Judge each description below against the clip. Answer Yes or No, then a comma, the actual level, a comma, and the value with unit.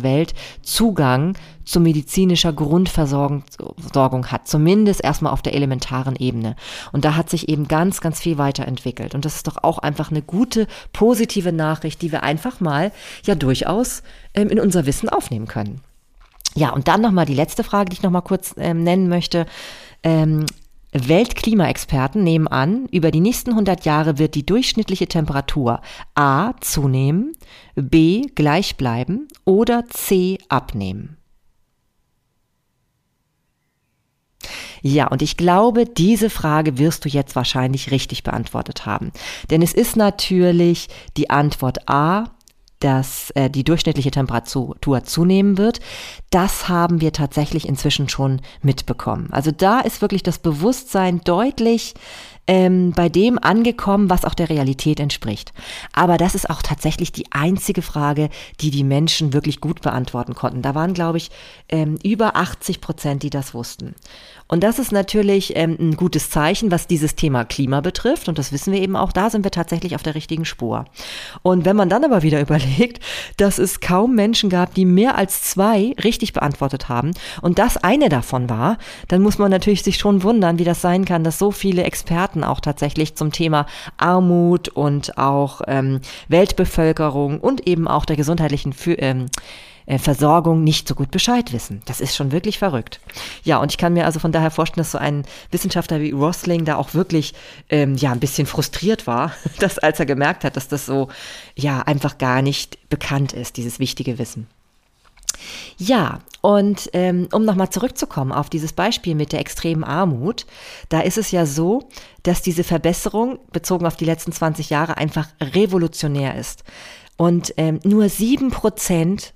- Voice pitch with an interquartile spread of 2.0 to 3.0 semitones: No, average, 4.8 semitones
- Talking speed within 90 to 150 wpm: No, average, 160 wpm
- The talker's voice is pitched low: No, medium, 160 Hz